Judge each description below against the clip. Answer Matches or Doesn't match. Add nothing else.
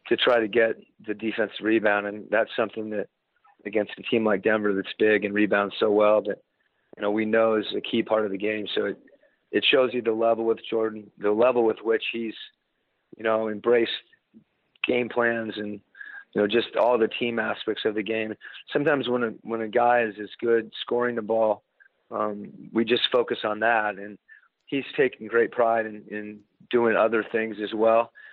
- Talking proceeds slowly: Doesn't match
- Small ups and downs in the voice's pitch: Matches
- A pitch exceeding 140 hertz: Doesn't match